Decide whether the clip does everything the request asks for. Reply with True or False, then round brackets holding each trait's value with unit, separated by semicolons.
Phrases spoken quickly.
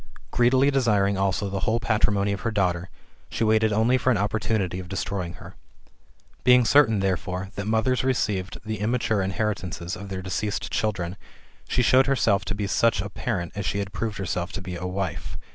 False (185 wpm)